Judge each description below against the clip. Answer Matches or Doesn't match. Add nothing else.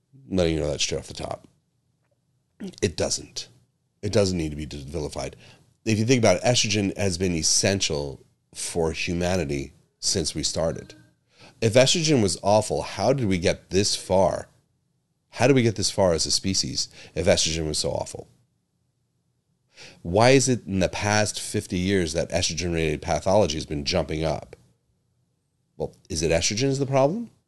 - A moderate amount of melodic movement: Doesn't match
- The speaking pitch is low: Matches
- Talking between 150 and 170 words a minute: Matches